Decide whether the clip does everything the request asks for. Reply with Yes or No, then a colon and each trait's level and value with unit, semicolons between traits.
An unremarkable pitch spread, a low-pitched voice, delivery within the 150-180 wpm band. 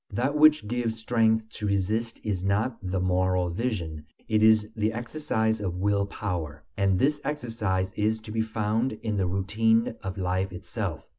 Yes: average, 3.2 semitones; low, 105 Hz; average, 165 wpm